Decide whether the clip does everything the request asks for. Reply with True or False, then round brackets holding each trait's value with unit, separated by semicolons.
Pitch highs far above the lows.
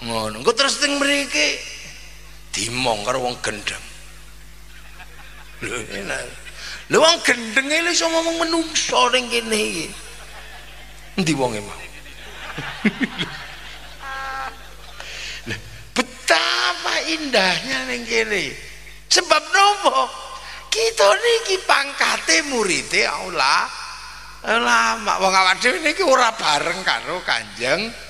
True (7.2 semitones)